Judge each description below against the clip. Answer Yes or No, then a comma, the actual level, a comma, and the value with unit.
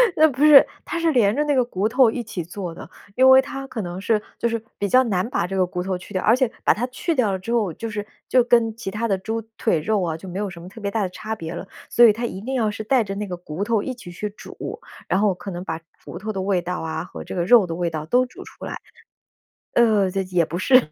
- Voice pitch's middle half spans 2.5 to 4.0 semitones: No, average, 4.6 semitones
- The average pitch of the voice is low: No, high, 210 Hz